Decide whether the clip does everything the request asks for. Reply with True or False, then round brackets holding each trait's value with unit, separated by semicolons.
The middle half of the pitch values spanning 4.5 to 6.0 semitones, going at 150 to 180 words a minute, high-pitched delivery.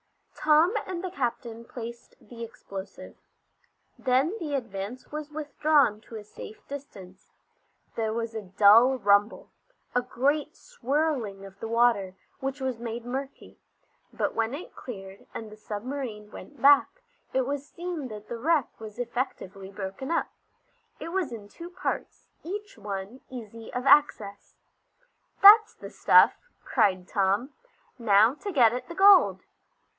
False (5.4 semitones; 140 wpm; 240 Hz)